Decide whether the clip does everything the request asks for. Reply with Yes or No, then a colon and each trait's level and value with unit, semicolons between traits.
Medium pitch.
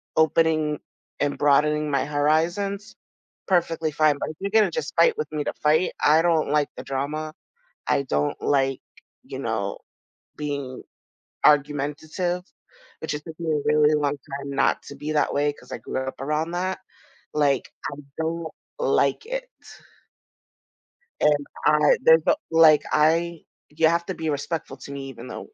Yes: medium, 150 Hz